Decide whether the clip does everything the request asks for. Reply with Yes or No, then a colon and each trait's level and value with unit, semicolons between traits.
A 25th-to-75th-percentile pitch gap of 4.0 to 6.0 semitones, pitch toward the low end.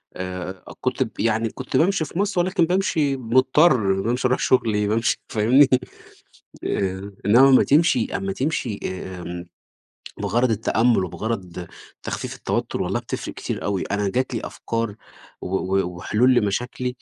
Yes: average, 5.0 semitones; low, 115 Hz